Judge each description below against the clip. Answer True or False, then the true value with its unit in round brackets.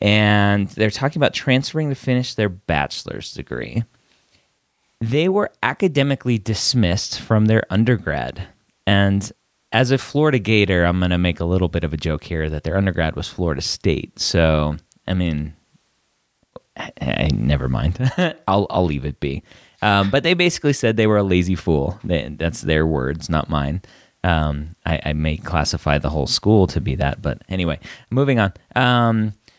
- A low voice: True (95 Hz)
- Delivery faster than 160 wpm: True (170 wpm)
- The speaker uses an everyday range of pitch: False (6.5 semitones)